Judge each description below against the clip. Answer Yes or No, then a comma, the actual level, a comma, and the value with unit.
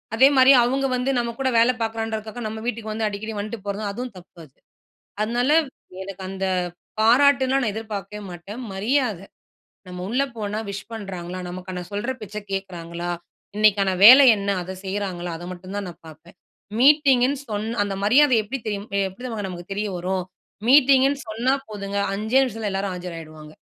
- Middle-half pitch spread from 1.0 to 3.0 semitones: No, average, 4.1 semitones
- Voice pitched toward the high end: Yes, high, 210 Hz